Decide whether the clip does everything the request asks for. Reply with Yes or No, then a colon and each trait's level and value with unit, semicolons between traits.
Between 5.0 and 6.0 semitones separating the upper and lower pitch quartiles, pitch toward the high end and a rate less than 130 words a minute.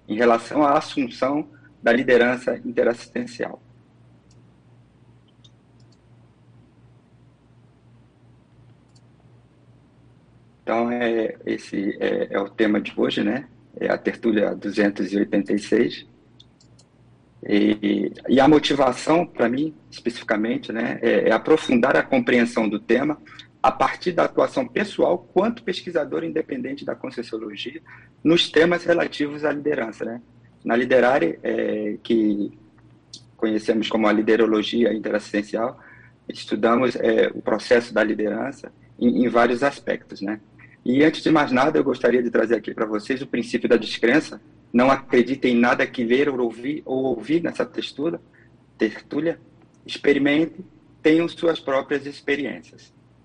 No: wide, 5.5 semitones; low, 120 Hz; slow, 120 wpm